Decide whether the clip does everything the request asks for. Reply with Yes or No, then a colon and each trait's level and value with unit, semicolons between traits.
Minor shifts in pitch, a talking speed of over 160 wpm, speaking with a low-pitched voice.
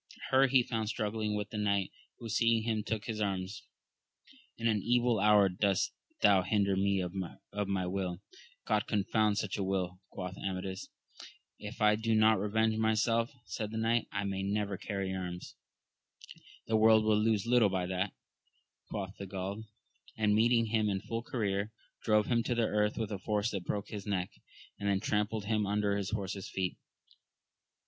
Yes: narrow, 2.2 semitones; average, 180 wpm; low, 105 Hz